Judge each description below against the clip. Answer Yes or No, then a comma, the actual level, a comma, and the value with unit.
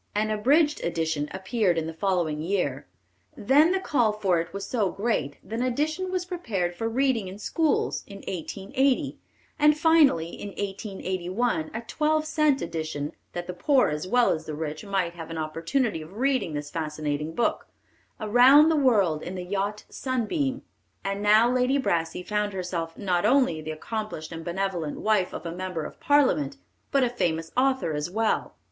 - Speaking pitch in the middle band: No, high, 200 Hz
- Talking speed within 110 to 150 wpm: No, average, 175 wpm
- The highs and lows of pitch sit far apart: Yes, wide, 7.4 semitones